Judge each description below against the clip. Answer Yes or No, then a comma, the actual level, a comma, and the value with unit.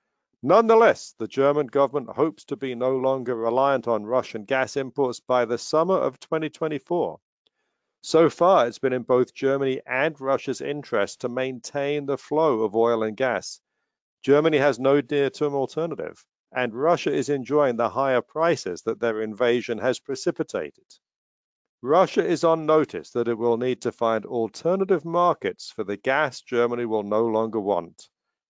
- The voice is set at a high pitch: No, low, 135 Hz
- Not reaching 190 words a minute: Yes, average, 155 wpm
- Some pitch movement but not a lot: Yes, average, 3.7 semitones